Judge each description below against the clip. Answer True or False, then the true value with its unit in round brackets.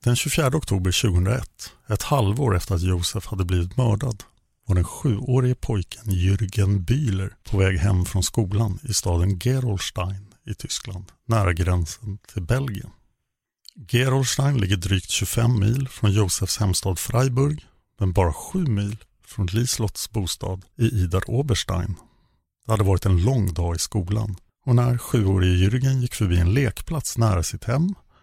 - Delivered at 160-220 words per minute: False (150 wpm)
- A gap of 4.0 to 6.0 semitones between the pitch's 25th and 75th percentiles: True (4.5 semitones)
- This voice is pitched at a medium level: False (105 Hz)